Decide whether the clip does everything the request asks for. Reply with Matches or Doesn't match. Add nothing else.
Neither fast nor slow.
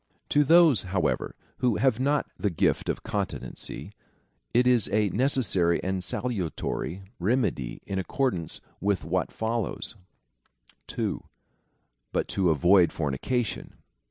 Doesn't match